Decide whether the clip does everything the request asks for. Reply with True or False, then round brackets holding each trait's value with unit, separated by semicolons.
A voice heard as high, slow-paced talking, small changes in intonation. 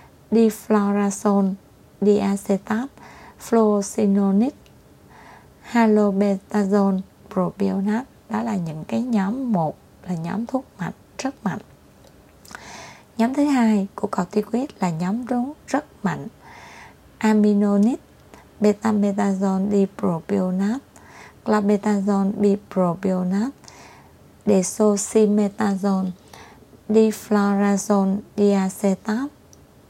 True (205 Hz; 70 wpm; 1.9 semitones)